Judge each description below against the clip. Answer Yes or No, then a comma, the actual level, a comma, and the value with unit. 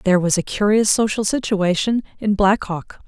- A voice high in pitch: Yes, high, 205 Hz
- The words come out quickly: No, average, 175 wpm